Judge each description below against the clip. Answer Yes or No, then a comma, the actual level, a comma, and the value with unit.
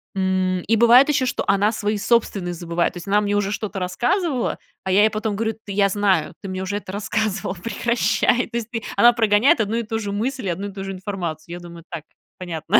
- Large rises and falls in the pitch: No, average, 3.2 semitones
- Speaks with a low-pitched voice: No, high, 205 Hz